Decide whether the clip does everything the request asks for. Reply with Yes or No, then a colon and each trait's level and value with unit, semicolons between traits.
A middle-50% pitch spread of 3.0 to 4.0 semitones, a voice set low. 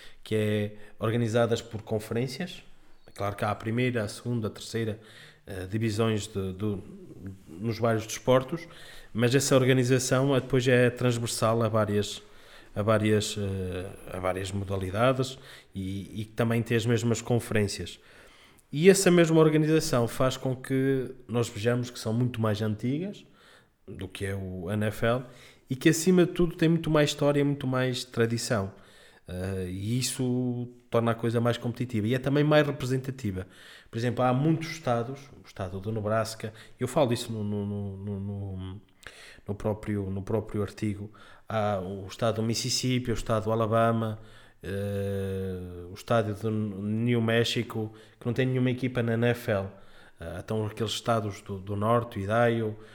Yes: average, 3.4 semitones; low, 115 Hz